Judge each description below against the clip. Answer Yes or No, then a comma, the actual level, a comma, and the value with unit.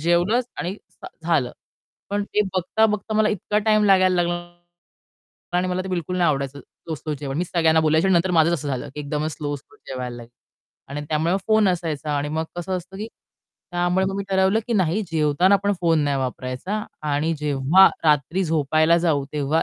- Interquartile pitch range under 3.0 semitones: No, average, 4.2 semitones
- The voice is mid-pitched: Yes, medium, 170 Hz